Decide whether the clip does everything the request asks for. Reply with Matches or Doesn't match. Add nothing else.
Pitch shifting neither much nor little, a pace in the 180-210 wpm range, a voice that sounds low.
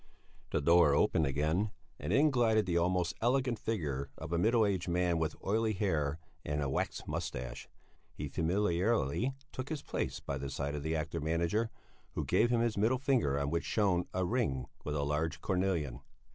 Doesn't match